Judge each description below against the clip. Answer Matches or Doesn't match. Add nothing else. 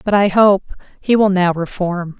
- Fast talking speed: Doesn't match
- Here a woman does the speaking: Matches